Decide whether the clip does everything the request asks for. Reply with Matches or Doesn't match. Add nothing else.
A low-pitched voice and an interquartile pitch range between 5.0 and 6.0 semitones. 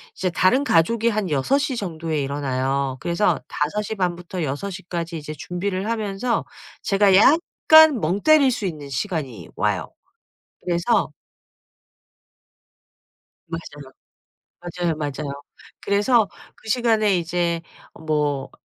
Doesn't match